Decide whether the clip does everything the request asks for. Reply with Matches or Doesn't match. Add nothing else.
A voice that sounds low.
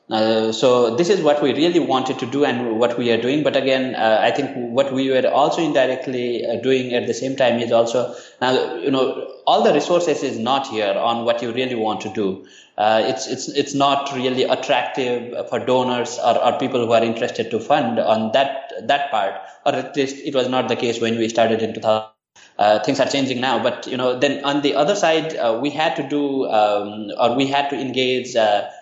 Matches